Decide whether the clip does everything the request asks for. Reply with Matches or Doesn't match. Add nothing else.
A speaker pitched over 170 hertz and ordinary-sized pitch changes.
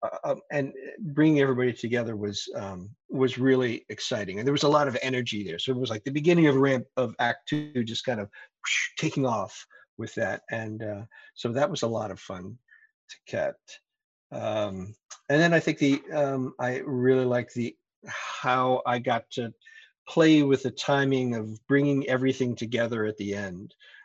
Doesn't match